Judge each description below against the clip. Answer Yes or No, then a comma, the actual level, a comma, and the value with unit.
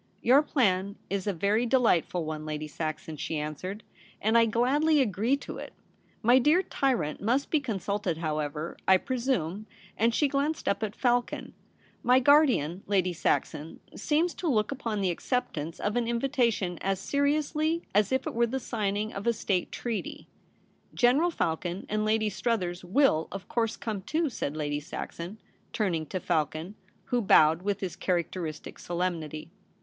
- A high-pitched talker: Yes, high, 205 Hz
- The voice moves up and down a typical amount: No, wide, 6.3 semitones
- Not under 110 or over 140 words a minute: No, average, 170 wpm